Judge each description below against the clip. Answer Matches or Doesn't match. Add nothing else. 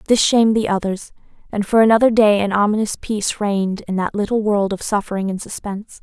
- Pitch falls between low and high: Doesn't match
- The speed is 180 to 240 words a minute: Matches